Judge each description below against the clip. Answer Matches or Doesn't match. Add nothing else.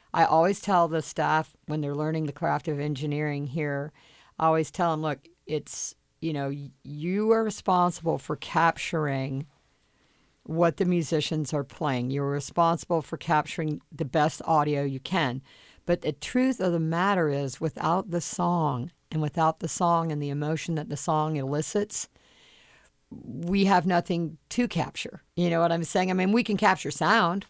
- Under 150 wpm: Doesn't match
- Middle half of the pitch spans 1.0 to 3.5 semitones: Matches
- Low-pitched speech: Doesn't match